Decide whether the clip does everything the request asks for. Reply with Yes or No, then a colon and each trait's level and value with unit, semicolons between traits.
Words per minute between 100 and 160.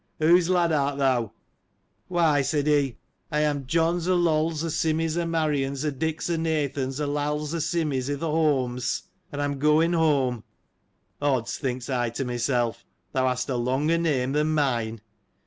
No: average, 175 wpm